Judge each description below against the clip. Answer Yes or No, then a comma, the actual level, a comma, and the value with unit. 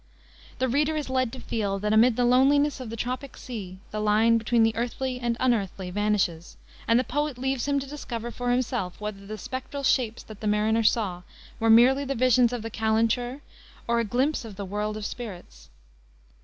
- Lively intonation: No, average, 3.3 semitones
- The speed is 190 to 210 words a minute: Yes, average, 200 wpm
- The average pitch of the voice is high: Yes, high, 235 Hz